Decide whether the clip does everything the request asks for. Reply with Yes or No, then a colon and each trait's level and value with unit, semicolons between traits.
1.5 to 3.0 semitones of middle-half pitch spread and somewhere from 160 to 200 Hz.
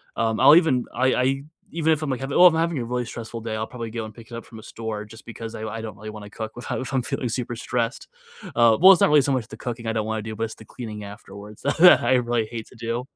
No: average, 2.7 semitones; low, 115 Hz